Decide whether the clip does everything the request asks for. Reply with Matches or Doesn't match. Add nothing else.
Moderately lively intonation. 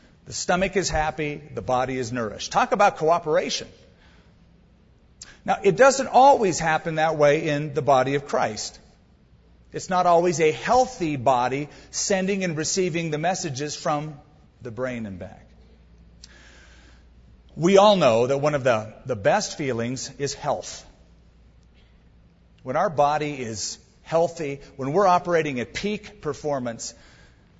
Doesn't match